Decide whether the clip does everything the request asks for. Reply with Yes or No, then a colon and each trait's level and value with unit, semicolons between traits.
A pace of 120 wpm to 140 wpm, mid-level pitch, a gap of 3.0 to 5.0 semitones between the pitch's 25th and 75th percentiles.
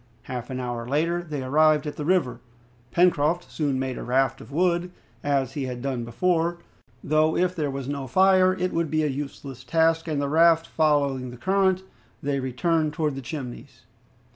No: average, 185 wpm; medium, 150 Hz; average, 4.1 semitones